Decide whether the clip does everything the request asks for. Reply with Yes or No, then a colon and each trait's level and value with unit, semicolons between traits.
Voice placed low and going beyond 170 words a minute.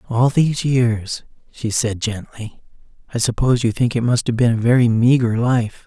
Yes: low, 120 Hz; average, 185 wpm